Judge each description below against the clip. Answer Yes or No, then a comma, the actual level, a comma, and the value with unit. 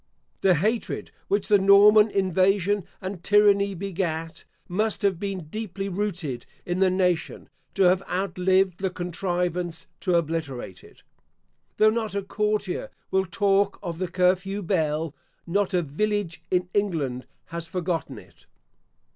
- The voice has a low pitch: No, medium, 185 Hz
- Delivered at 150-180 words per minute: No, slow, 135 wpm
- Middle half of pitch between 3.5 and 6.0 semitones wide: No, average, 2.8 semitones